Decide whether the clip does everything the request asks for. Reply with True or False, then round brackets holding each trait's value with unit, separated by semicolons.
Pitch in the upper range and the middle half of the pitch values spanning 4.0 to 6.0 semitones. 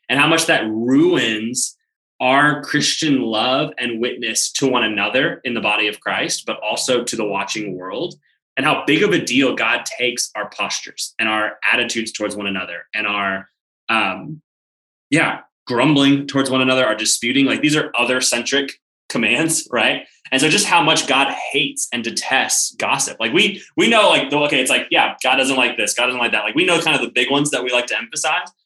False (125 Hz; 4.4 semitones)